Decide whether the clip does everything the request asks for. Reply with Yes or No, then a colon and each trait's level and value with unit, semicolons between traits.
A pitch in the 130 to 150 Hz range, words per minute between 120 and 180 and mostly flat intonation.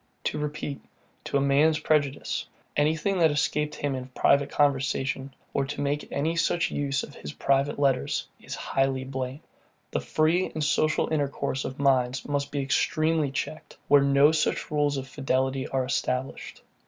Yes: medium, 140 Hz; average, 160 wpm; narrow, 2.0 semitones